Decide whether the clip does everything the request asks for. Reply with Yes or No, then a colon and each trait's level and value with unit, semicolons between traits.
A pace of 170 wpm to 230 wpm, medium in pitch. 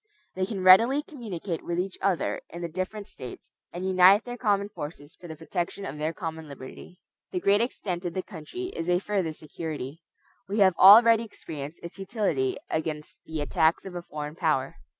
Yes: average, 185 wpm; medium, 180 Hz